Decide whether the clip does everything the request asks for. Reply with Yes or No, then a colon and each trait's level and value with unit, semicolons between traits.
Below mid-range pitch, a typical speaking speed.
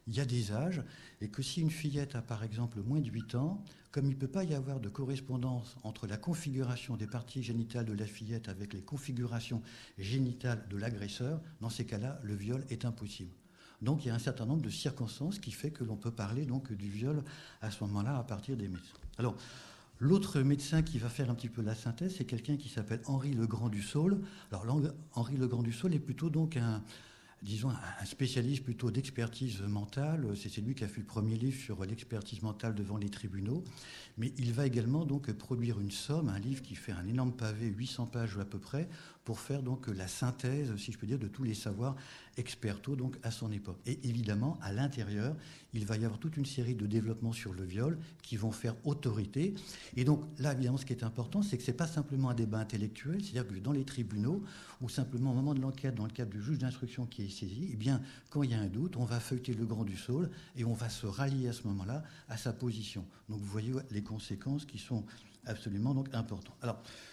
No: low, 120 Hz; fast, 230 wpm